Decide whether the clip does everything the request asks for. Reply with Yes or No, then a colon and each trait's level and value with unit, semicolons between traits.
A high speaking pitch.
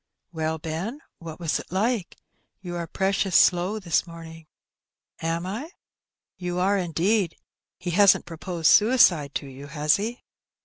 No: medium, 175 Hz